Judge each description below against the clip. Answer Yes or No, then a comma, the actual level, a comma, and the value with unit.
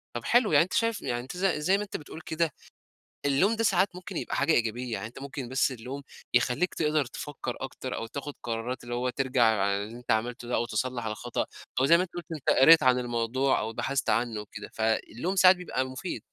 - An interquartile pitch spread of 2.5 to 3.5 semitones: No, average, 5.3 semitones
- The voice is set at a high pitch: No, low, 130 Hz